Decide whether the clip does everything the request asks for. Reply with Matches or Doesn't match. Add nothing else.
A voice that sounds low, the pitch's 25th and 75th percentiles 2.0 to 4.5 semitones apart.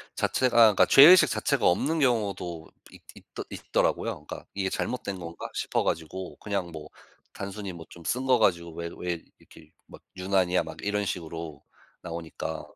Matches